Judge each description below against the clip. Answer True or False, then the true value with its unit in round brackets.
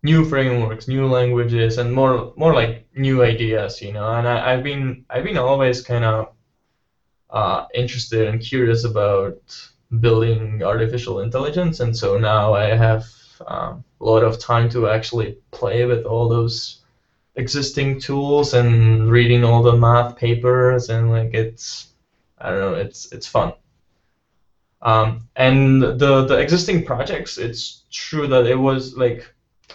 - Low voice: True (120 Hz)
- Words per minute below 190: True (145 wpm)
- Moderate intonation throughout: False (2.3 semitones)